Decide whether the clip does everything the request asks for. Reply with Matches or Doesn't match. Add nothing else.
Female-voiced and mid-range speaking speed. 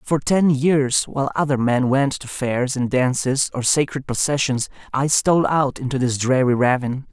Doesn't match